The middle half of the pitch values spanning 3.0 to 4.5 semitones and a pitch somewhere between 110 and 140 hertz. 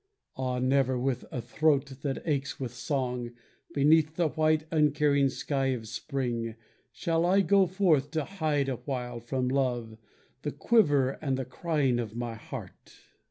Yes: average, 3.7 semitones; low, 135 Hz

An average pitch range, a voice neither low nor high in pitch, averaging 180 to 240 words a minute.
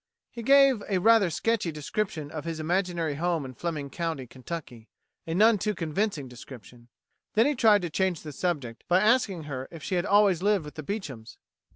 No: wide, 5.8 semitones; medium, 170 Hz; average, 190 wpm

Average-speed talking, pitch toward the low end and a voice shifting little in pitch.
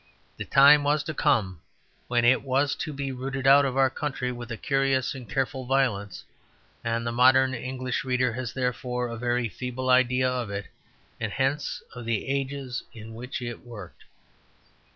Yes: average, 175 wpm; low, 125 Hz; narrow, 2.1 semitones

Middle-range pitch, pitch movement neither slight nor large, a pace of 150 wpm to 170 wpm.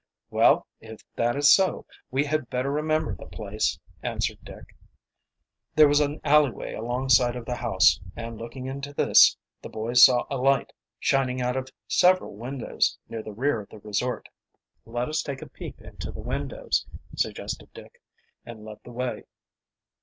No: low, 125 Hz; average, 3.4 semitones; average, 165 wpm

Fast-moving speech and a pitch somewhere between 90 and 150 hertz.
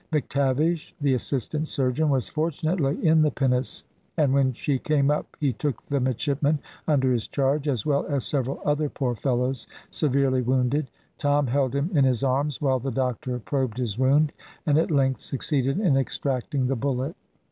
No: average, 170 wpm; low, 135 Hz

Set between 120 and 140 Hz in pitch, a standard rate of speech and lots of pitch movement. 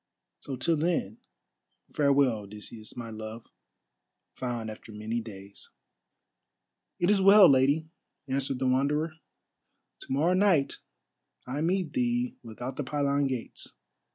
No: low, 135 Hz; slow, 120 wpm; wide, 5.7 semitones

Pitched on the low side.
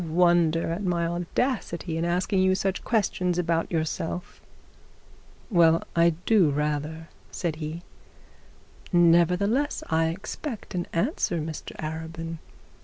No: medium, 170 Hz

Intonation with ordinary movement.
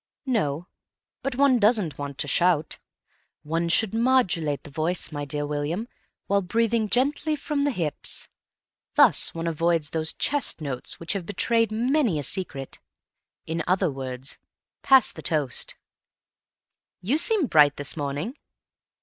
No: wide, 7.9 semitones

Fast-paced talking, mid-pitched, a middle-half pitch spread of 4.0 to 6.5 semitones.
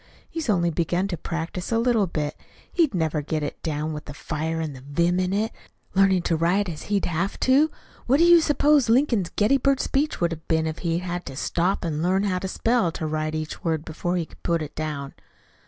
Yes: fast, 225 wpm; medium, 175 Hz; average, 4.5 semitones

